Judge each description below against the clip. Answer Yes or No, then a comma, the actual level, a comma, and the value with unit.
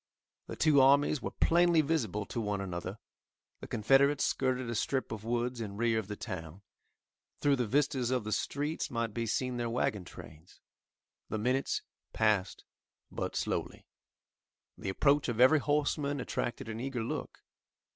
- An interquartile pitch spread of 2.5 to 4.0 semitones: No, average, 4.5 semitones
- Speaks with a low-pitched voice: Yes, low, 120 Hz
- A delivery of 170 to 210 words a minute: No, average, 155 wpm